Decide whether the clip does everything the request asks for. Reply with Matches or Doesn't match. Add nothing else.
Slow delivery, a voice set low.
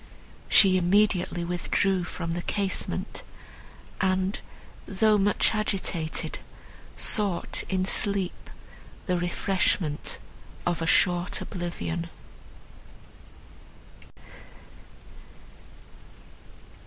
Doesn't match